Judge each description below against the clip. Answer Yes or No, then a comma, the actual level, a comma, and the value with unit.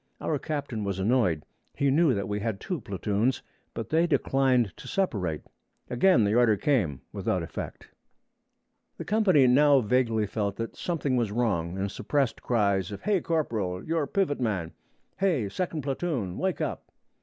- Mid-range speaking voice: No, low, 120 Hz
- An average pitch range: No, wide, 6.6 semitones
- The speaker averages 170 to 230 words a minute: No, average, 155 wpm